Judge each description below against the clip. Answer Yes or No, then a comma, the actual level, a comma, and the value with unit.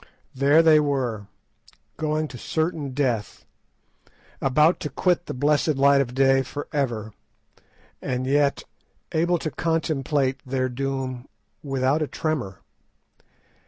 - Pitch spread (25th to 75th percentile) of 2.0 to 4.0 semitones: Yes, average, 3.0 semitones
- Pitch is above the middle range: No, medium, 140 Hz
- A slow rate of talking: Yes, slow, 115 wpm